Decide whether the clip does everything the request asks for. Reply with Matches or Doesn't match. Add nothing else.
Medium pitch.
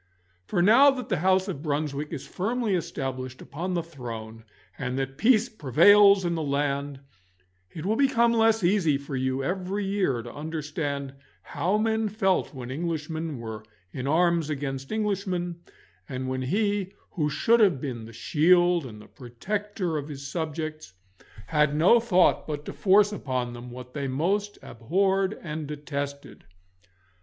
Matches